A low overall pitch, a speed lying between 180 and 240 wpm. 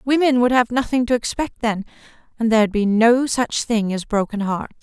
No: high, 230 Hz; average, 200 wpm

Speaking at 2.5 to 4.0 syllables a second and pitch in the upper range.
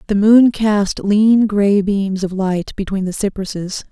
Yes: 3.9 syllables/s; high, 200 Hz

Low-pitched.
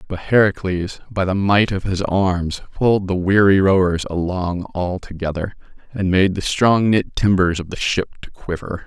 Yes: very low, 95 Hz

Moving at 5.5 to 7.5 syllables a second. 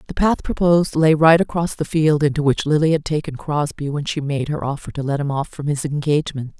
Yes: 5.6 syllables/s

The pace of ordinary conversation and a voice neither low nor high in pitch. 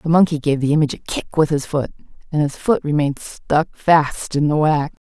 No: fast, 225 wpm; medium, 150 Hz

